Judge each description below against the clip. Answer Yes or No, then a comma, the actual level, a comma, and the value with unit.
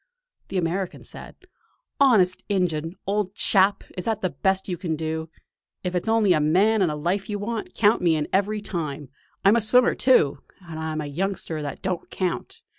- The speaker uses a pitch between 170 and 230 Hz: Yes, medium, 185 Hz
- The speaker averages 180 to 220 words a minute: Yes, average, 190 wpm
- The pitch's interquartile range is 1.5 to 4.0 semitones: No, average, 4.4 semitones